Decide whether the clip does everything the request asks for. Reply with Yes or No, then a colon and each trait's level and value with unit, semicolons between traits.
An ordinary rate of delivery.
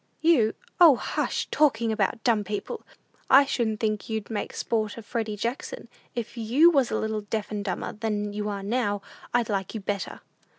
Yes: average, 185 wpm